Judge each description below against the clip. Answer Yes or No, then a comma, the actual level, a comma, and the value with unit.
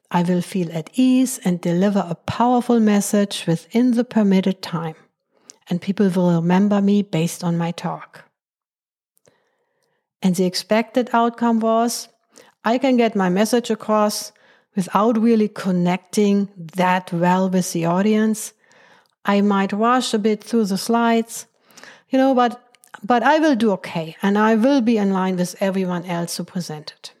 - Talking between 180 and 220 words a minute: No, average, 150 wpm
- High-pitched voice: Yes, high, 205 Hz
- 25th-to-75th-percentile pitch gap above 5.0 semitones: No, average, 4.2 semitones